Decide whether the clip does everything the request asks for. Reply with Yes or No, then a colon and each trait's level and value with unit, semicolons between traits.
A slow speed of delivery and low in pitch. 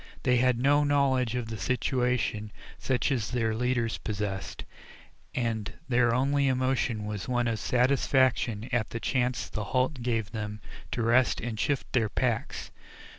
No: average, 155 wpm; low, 120 Hz